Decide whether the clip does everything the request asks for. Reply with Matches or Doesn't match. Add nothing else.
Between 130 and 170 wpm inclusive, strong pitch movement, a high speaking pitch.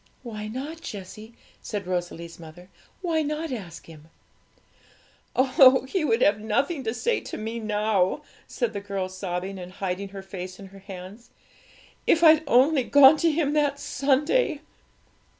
Matches